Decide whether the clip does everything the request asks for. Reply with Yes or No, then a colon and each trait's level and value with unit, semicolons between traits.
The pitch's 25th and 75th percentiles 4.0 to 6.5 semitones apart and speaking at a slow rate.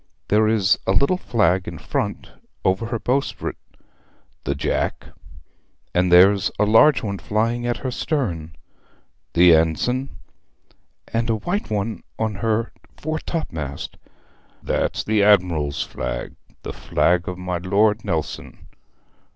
Yes: average, 4.7 semitones; slow, 125 wpm